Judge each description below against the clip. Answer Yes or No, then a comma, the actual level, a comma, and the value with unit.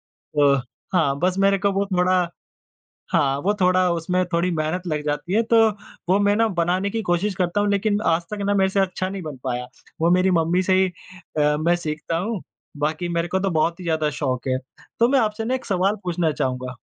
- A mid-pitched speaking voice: Yes, medium, 180 Hz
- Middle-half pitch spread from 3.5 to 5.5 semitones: Yes, average, 3.9 semitones